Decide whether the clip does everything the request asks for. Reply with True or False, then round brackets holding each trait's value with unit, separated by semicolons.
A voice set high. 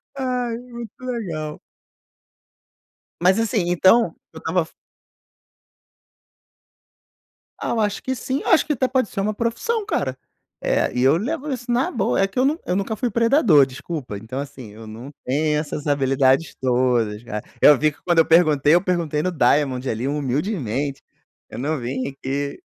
False (160 Hz)